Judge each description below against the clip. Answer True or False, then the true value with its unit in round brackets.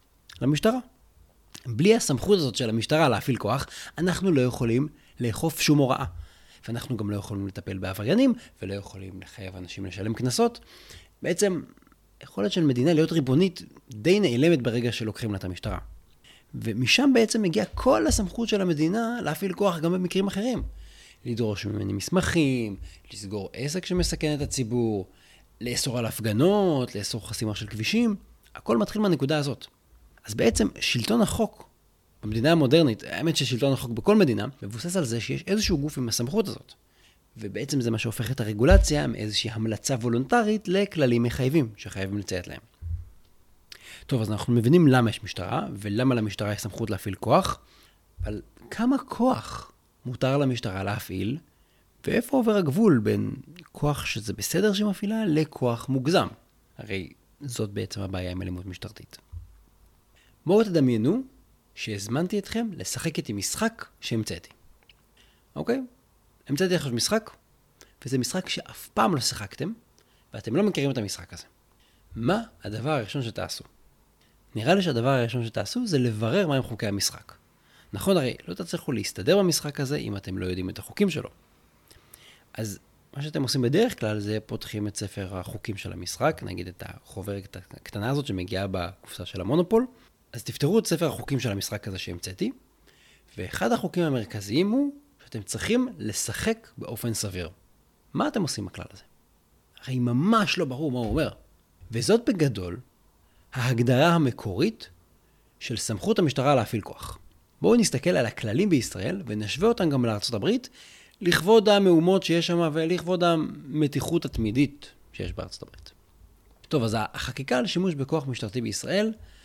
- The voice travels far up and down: True (8.5 semitones)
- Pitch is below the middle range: True (125 Hz)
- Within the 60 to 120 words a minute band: False (140 wpm)